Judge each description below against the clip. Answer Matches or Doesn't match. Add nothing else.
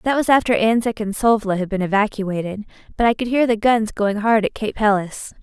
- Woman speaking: Matches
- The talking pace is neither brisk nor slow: Doesn't match